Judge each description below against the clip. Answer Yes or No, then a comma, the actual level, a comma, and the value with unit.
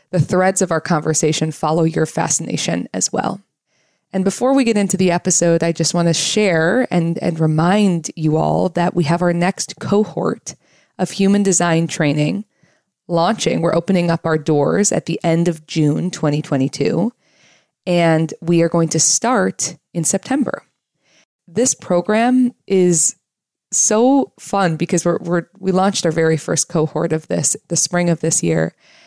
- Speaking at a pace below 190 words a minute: Yes, average, 160 wpm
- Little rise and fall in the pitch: No, average, 3.0 semitones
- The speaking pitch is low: No, medium, 170 Hz